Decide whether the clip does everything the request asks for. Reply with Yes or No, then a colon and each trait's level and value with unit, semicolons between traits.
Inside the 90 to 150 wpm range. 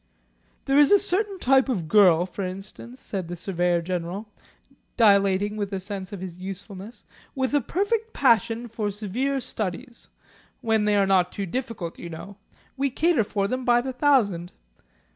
No: average, 165 wpm